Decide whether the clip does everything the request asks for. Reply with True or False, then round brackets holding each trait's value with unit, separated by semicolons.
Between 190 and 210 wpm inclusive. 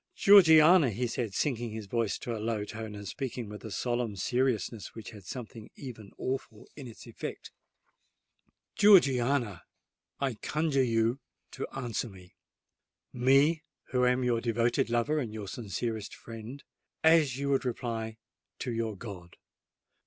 False (135 wpm)